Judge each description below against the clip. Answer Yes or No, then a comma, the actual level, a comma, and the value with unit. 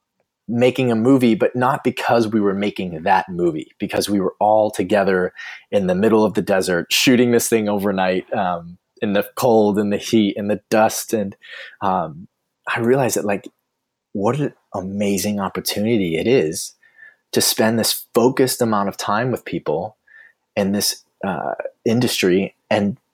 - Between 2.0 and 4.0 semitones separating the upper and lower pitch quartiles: Yes, average, 2.9 semitones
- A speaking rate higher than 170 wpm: No, average, 160 wpm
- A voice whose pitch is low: Yes, low, 105 Hz